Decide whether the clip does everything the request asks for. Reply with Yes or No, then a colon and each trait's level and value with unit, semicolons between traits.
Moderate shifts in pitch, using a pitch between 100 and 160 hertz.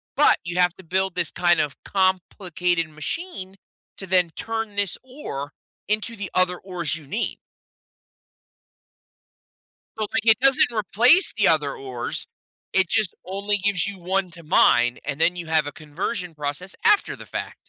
No: average, 3.9 semitones; medium, 185 Hz